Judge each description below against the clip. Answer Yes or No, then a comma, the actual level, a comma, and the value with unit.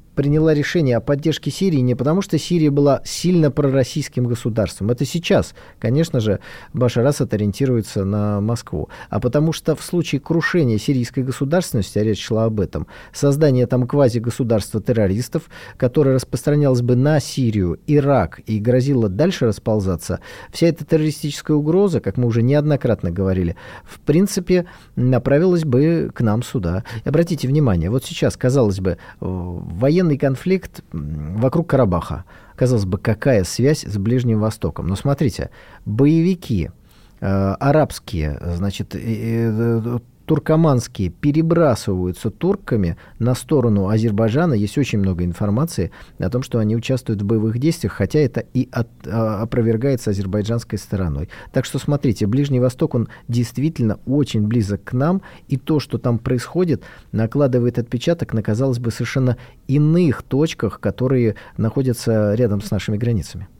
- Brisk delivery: No, average, 140 wpm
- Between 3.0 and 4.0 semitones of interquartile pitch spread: No, average, 5.3 semitones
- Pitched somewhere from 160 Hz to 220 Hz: No, low, 125 Hz